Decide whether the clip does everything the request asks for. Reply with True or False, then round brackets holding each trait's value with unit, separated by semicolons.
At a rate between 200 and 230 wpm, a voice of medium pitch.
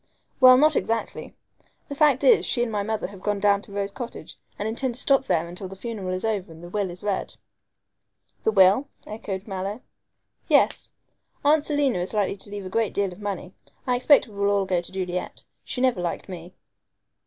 False (205 wpm; 205 Hz)